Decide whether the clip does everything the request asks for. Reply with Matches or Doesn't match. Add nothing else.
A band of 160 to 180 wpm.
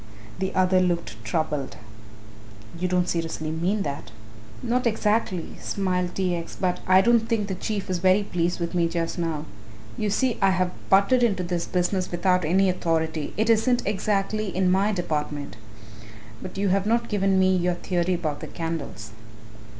Matches